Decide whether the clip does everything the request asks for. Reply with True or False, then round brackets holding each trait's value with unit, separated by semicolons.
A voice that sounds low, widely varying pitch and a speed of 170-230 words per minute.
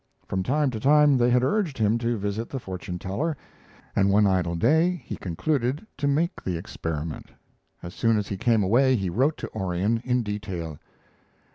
True (115 Hz; 6.1 semitones; 180 wpm)